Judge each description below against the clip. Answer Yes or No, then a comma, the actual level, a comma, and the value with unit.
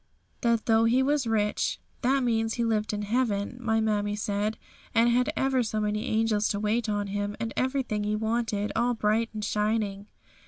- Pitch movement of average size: No, narrow, 2.1 semitones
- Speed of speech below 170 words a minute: No, average, 190 wpm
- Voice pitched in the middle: No, high, 220 Hz